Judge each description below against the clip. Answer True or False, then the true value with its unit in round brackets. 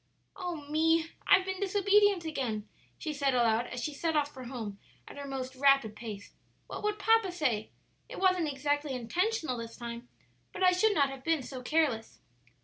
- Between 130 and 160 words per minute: False (180 wpm)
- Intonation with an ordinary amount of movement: False (6.4 semitones)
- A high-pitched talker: True (290 Hz)